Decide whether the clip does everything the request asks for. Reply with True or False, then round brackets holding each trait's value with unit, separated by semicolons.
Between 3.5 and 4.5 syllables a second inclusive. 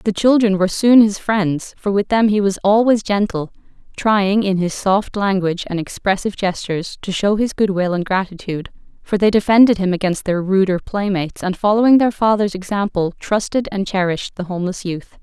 False (5.5 syllables/s)